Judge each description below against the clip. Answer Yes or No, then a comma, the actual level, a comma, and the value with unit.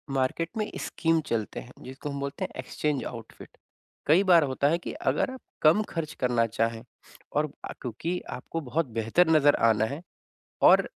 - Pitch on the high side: No, medium, 145 Hz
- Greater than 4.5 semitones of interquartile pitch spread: Yes, average, 5.1 semitones